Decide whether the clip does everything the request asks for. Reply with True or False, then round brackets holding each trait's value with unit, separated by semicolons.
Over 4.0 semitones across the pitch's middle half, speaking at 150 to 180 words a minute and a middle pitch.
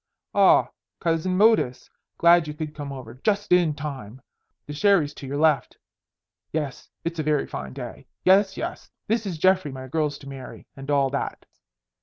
True (4.5 semitones; 170 wpm; 150 Hz)